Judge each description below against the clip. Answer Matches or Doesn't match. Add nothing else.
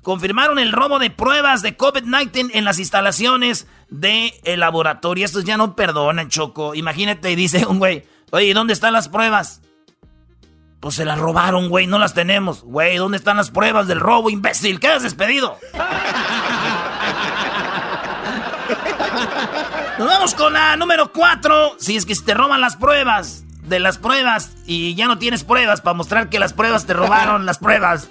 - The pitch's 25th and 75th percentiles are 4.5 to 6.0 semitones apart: Matches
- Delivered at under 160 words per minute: Doesn't match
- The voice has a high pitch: Matches